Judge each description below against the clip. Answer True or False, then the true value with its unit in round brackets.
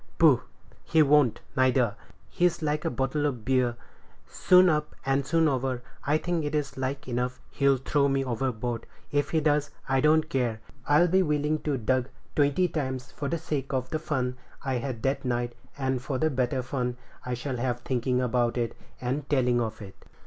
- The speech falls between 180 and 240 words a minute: True (190 wpm)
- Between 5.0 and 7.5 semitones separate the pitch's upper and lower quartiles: False (3.0 semitones)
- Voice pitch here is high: False (135 Hz)